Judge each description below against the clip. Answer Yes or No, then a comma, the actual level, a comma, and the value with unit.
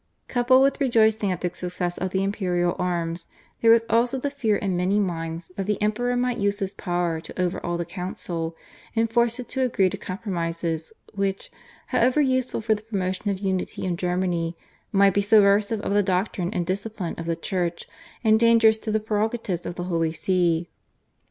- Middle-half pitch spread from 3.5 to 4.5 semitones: Yes, average, 3.9 semitones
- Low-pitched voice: No, high, 195 Hz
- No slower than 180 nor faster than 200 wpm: Yes, average, 185 wpm